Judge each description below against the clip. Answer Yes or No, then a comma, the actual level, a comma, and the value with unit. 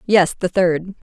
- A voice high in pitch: No, medium, 180 Hz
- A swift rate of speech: No, average, 165 wpm